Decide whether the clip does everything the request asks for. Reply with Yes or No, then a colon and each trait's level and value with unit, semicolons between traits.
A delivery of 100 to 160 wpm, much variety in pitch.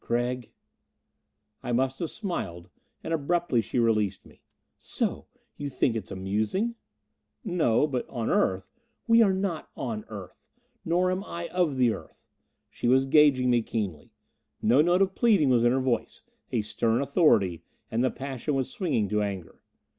No: average, 170 wpm; wide, 7.2 semitones